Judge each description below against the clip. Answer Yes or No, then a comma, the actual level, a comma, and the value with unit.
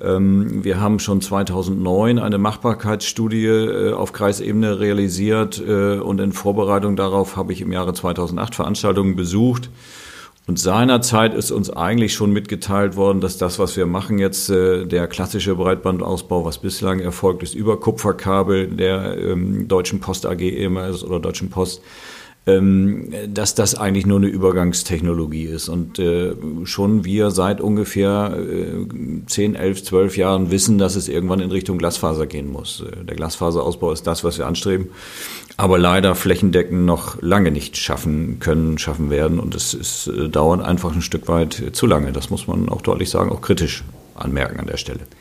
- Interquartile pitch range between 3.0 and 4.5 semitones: No, narrow, 2.4 semitones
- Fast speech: No, average, 150 wpm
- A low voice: Yes, very low, 95 Hz